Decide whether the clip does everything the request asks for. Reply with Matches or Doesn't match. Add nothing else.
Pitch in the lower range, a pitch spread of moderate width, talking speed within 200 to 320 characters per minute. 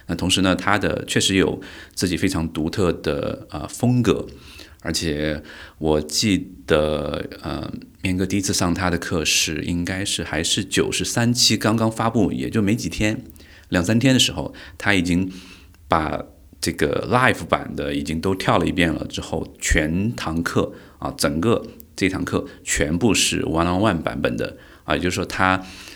Matches